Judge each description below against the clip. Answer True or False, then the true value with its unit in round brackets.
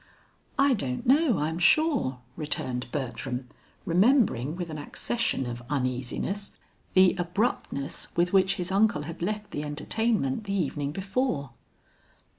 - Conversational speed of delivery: False (130 wpm)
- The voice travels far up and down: True (7.0 semitones)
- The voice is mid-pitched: True (170 Hz)